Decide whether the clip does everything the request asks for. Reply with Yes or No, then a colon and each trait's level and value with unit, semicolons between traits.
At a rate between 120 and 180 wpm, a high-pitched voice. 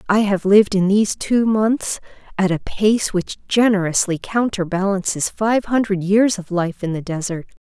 Yes: average, 165 wpm; high, 200 Hz